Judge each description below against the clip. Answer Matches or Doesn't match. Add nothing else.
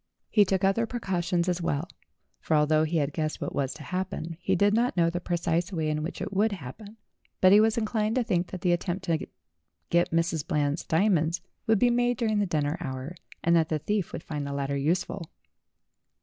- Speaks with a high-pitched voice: Doesn't match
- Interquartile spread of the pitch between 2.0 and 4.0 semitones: Doesn't match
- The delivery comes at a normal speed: Doesn't match